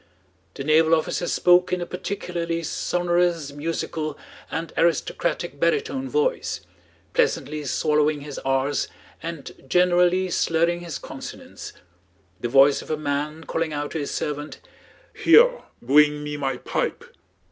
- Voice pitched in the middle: Yes, medium, 160 Hz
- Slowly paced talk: Yes, slow, 125 wpm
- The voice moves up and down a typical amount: Yes, average, 3.2 semitones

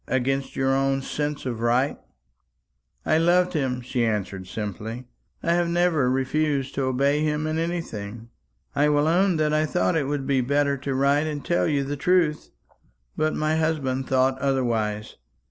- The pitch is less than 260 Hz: Yes, medium, 140 Hz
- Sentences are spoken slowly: No, average, 165 wpm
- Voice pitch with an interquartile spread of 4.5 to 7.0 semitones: No, average, 3.2 semitones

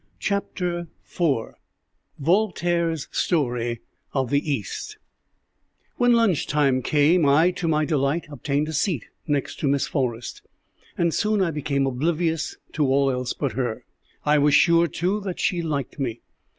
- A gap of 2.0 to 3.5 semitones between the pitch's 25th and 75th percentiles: No, average, 4.0 semitones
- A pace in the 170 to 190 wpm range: No, average, 145 wpm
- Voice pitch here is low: No, medium, 150 Hz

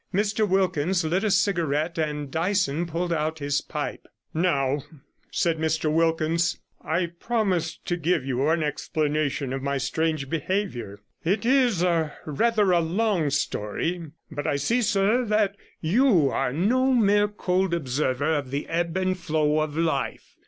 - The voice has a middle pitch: Yes, medium, 165 Hz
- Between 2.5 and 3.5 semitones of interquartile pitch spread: No, average, 4.5 semitones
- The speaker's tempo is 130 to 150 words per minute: Yes, average, 145 wpm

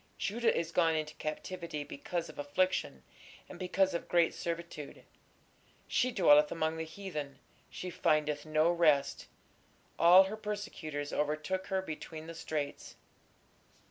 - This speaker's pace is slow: Yes, slow, 130 wpm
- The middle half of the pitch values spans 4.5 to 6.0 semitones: No, average, 3.3 semitones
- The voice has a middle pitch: Yes, medium, 165 Hz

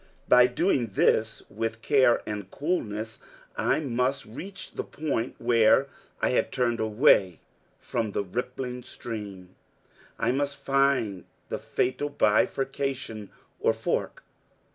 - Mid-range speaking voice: No, low, 120 Hz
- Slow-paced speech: Yes, slow, 120 wpm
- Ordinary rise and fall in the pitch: Yes, average, 4.1 semitones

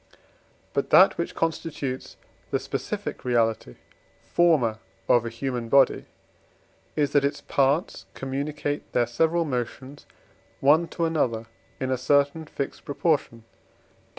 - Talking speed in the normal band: No, slow, 125 wpm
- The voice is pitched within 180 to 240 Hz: No, medium, 140 Hz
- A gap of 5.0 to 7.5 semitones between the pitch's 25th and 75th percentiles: No, average, 3.7 semitones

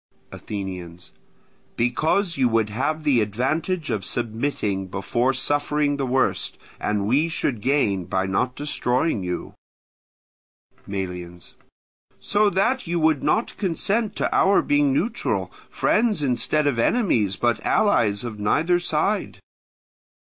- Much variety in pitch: Yes, wide, 7.5 semitones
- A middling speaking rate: No, slow, 120 wpm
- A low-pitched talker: Yes, low, 130 Hz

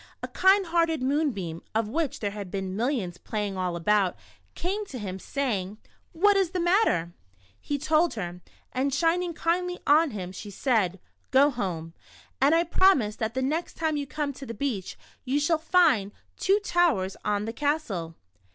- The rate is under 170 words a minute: No, average, 185 wpm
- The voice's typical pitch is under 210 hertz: No, very high, 265 Hz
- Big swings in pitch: Yes, wide, 8.5 semitones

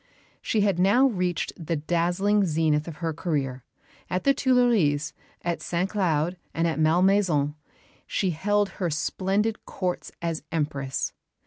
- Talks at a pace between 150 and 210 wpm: No, slow, 135 wpm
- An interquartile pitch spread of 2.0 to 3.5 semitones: No, average, 4.1 semitones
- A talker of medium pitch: Yes, medium, 175 Hz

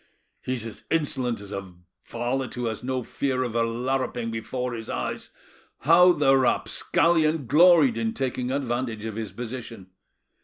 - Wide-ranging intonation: No, average, 2.8 semitones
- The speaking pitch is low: Yes, low, 125 Hz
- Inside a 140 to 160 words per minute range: Yes, average, 150 wpm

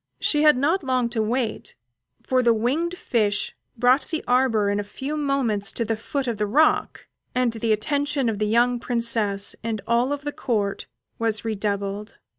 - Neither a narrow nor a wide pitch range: Yes, average, 3.8 semitones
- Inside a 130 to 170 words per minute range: No, average, 180 wpm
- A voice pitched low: No, high, 235 Hz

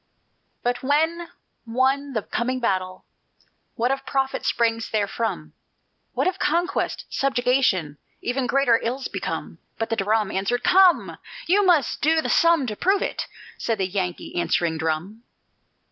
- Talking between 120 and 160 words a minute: Yes, average, 140 wpm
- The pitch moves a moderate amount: No, wide, 5.8 semitones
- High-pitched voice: Yes, high, 245 Hz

